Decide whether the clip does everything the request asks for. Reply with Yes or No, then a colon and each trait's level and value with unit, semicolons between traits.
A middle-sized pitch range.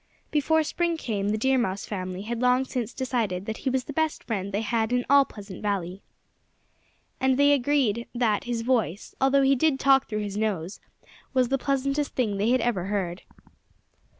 Yes: average, 4.7 semitones